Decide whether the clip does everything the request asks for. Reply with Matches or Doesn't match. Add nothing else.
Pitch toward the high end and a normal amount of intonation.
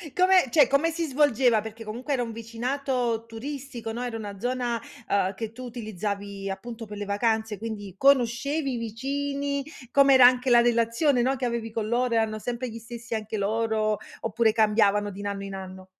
Matches